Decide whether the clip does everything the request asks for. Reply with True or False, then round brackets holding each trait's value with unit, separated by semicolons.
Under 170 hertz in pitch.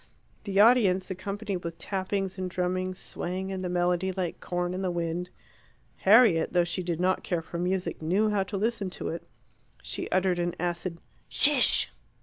False (185 Hz)